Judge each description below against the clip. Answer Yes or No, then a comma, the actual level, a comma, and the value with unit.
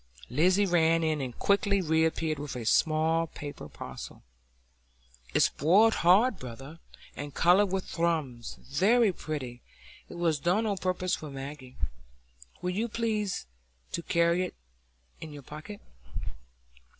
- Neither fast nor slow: No, slow, 130 wpm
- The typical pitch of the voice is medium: Yes, medium, 165 Hz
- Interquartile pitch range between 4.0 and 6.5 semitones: Yes, average, 4.4 semitones